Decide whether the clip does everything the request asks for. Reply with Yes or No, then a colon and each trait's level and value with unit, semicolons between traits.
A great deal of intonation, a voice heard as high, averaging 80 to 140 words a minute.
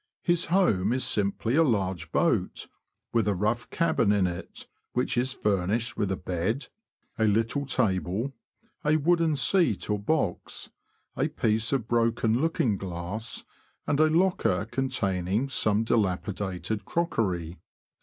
No: wide, 5.7 semitones; low, 110 Hz; slow, 135 wpm